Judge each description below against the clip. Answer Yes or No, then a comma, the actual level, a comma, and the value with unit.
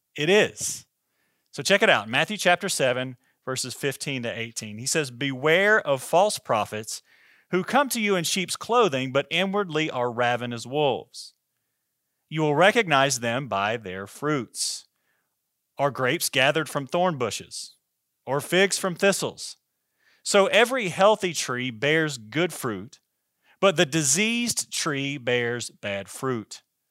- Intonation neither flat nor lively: No, wide, 6.7 semitones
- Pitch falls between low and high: Yes, medium, 145 Hz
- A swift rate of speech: No, average, 140 wpm